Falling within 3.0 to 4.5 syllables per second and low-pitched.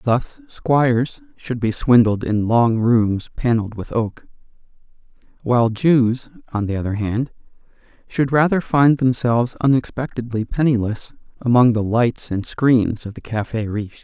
Yes: 4.4 syllables/s; low, 120 Hz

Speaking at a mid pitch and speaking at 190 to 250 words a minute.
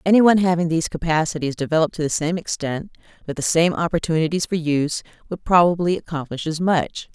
No: medium, 165 Hz; average, 175 wpm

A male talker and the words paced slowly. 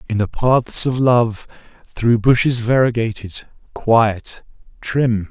Yes: male; slow, 115 wpm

